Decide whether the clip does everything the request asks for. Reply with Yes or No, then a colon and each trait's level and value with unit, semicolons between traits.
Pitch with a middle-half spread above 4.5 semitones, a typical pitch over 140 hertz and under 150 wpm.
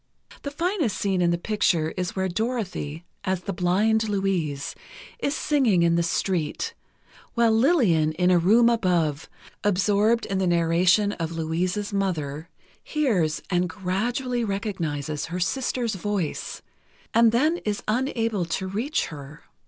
Yes: average, 4.9 semitones; high, 190 Hz; slow, 135 wpm